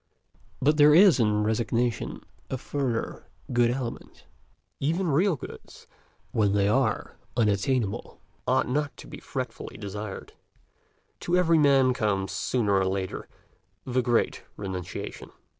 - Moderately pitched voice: No, low, 120 Hz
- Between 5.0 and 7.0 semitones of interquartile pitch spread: Yes, wide, 5.4 semitones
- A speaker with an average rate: No, slow, 125 wpm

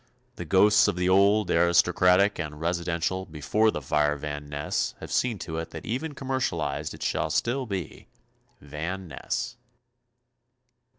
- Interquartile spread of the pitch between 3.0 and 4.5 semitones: No, wide, 5.4 semitones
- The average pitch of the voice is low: Yes, very low, 90 Hz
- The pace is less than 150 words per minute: Yes, average, 140 wpm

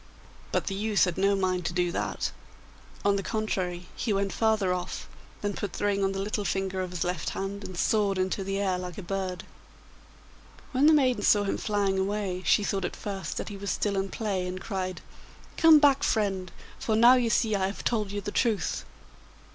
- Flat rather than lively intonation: Yes, narrow, 2.1 semitones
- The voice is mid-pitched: No, high, 195 Hz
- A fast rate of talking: Yes, fast, 210 wpm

